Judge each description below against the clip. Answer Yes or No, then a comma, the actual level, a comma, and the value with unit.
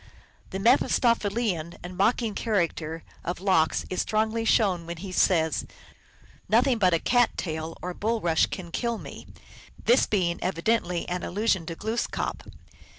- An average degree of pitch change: Yes, average, 4.7 semitones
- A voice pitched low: No, high, 190 Hz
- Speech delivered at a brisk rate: No, average, 145 wpm